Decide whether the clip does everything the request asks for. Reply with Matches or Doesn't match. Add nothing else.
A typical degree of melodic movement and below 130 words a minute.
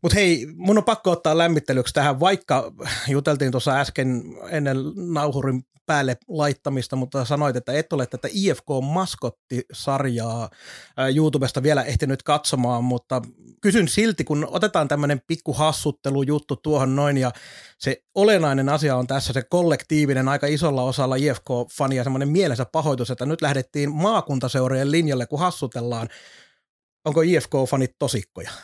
Doesn't match